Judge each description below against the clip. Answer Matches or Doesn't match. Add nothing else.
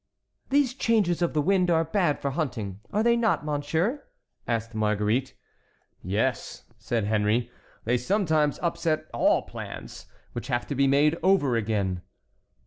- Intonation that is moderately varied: Doesn't match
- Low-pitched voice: Doesn't match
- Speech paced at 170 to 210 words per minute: Doesn't match